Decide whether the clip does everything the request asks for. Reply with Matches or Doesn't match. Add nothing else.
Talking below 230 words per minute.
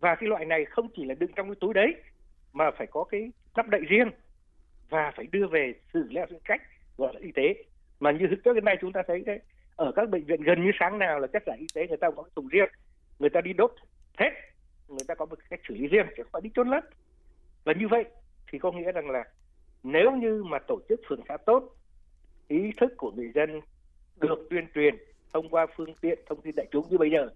Doesn't match